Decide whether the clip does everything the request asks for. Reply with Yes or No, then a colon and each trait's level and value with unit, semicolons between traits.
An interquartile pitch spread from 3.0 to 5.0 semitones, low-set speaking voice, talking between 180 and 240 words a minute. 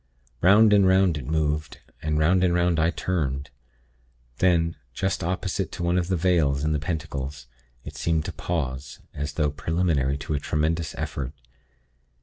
No: average, 3.3 semitones; very low, 80 Hz; average, 160 wpm